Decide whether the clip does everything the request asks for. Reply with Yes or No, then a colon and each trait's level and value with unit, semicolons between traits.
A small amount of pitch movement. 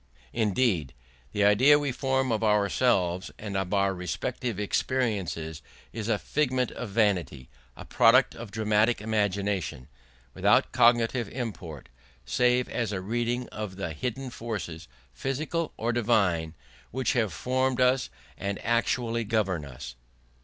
No: average, 4.2 semitones